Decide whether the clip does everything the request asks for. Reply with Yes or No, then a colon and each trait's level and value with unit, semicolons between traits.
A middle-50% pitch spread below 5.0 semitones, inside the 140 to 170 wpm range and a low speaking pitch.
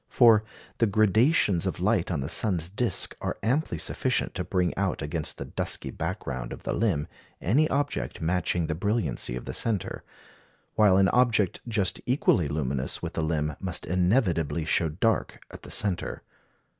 No: wide, 5.4 semitones; average, 165 wpm; very low, 95 Hz